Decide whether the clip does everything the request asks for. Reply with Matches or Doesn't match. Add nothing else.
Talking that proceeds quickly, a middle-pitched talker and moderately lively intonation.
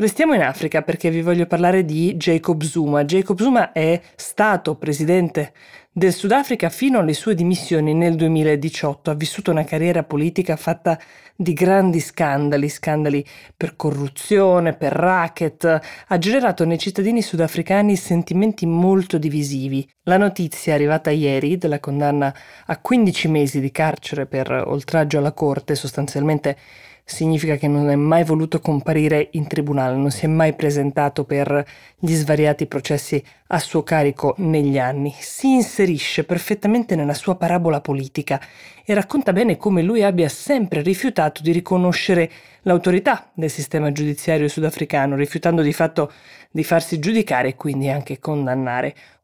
Doesn't match